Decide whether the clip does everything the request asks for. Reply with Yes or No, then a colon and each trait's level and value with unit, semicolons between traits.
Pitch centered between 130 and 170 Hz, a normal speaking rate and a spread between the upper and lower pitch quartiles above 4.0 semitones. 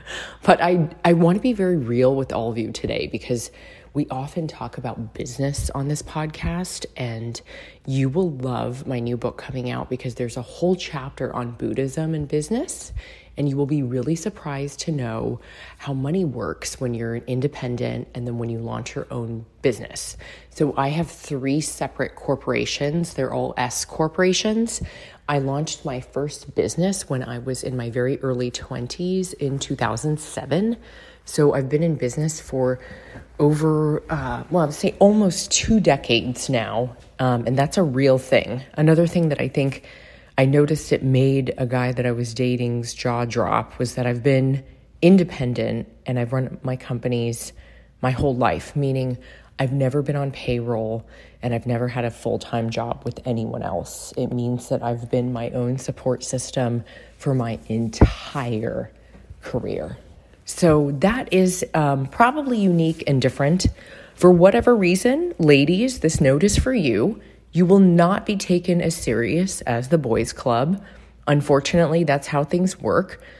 Yes: low, 135 Hz; average, 165 wpm; average, 4.8 semitones